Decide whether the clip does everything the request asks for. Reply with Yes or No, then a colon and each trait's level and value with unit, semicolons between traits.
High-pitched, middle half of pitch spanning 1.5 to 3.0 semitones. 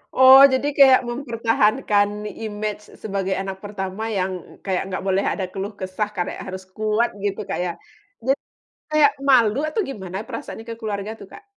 No: high, 210 Hz; average, 3.8 semitones